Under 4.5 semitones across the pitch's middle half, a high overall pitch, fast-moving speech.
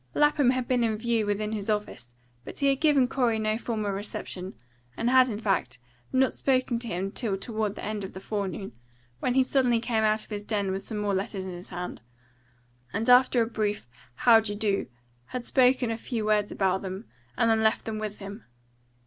Yes: average, 3.1 semitones; high, 220 Hz; fast, 210 wpm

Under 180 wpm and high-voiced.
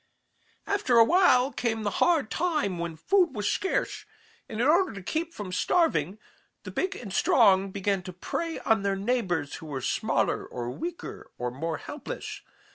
Yes: average, 170 wpm; high, 220 Hz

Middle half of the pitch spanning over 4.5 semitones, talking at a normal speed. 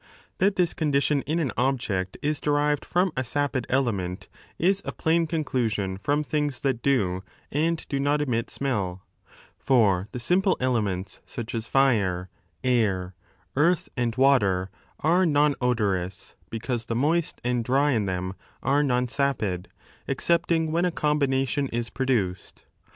Yes: average, 5.3 semitones; average, 145 wpm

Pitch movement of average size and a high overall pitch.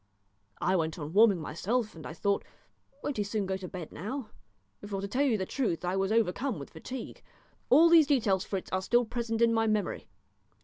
Yes: average, 4.1 semitones; high, 205 Hz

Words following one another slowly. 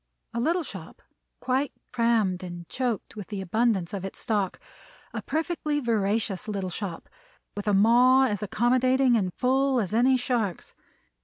No: average, 150 wpm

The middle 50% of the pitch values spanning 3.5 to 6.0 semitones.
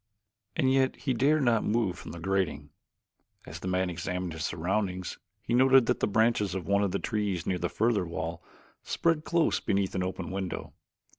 Yes: average, 4.6 semitones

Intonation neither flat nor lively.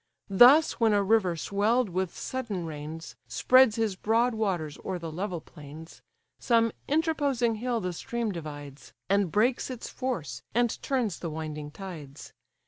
No: wide, 6.6 semitones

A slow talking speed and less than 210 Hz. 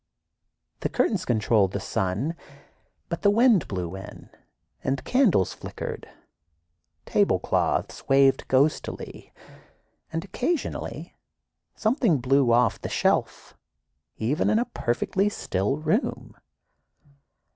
Yes: slow, 100 wpm; medium, 140 Hz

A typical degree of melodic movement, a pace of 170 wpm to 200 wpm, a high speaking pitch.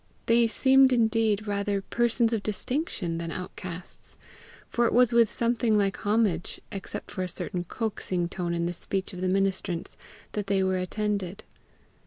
No: average, 3.8 semitones; average, 160 wpm; high, 200 Hz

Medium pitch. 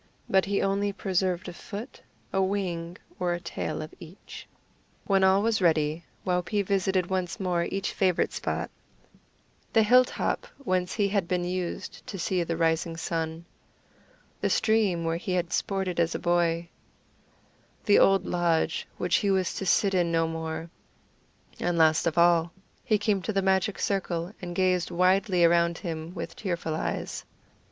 Yes: medium, 180 Hz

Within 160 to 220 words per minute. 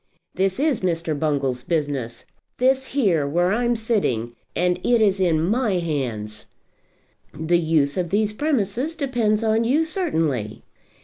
No: slow, 135 wpm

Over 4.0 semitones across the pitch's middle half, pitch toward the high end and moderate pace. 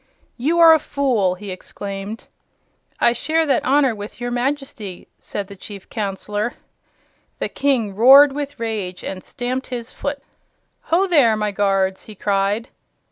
Yes: wide, 5.5 semitones; high, 230 Hz; average, 145 wpm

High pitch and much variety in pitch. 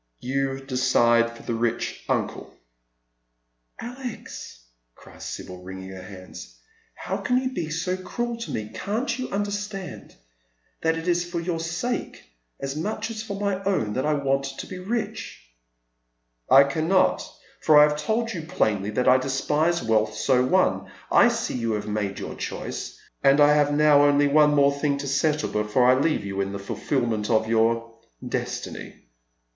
No: low, 135 Hz; wide, 8.3 semitones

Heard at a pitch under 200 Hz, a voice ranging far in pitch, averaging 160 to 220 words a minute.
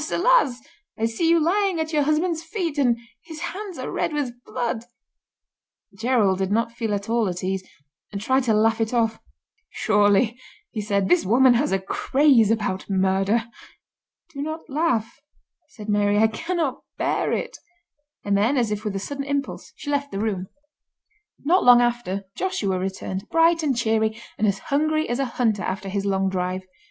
No: high, 230 Hz; wide, 6.2 semitones; average, 175 wpm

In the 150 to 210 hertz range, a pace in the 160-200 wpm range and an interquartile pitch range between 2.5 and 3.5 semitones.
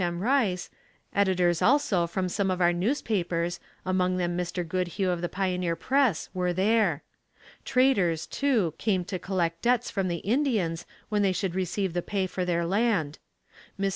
Yes: medium, 185 Hz; average, 165 wpm; average, 2.9 semitones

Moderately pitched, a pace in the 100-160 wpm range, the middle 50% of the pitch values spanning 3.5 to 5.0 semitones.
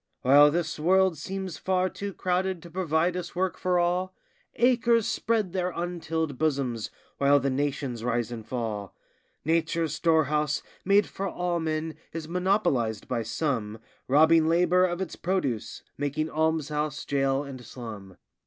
Yes: medium, 160 Hz; average, 145 wpm; average, 4.7 semitones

